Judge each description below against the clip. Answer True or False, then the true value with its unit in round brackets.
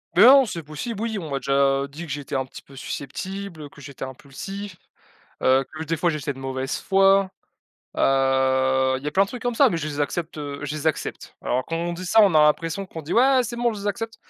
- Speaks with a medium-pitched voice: True (155 Hz)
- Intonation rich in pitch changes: True (6.3 semitones)